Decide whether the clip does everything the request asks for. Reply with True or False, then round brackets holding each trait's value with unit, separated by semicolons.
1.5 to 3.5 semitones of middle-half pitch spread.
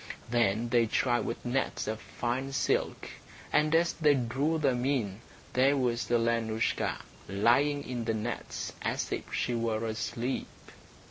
True (2.8 semitones)